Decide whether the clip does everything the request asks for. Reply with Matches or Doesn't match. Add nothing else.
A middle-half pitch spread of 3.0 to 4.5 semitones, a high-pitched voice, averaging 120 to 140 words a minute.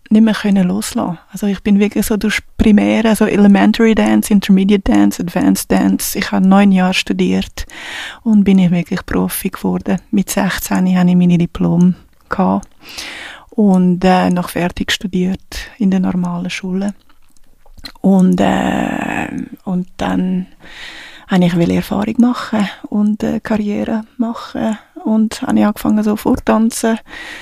Matches